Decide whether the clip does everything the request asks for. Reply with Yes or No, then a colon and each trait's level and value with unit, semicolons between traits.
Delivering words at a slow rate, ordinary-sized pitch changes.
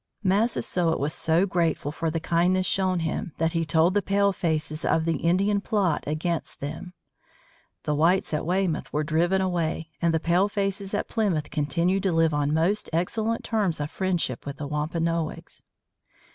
No: average, 160 wpm; average, 3.2 semitones